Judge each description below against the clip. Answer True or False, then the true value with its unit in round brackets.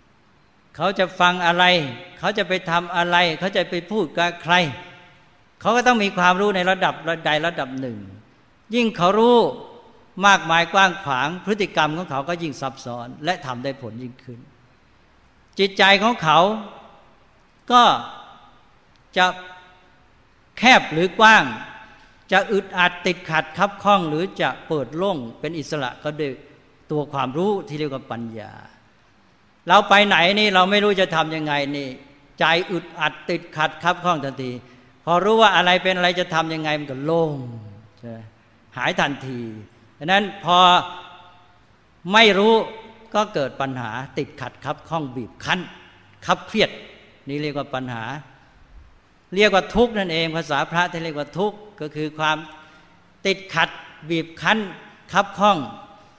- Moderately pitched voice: True (170 Hz)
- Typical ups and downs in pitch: False (5.7 semitones)